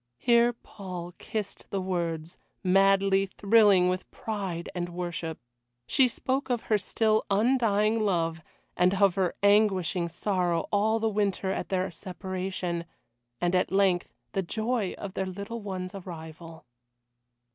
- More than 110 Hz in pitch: Yes, high, 190 Hz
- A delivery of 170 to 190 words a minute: No, slow, 135 wpm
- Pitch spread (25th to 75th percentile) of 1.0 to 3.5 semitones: Yes, average, 2.9 semitones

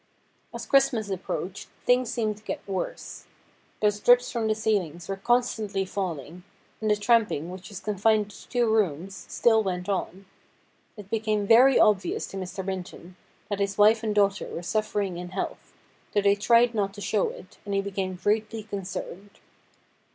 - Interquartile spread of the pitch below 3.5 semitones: Yes, narrow, 2.4 semitones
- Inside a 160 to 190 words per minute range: Yes, average, 165 wpm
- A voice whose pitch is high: Yes, high, 205 Hz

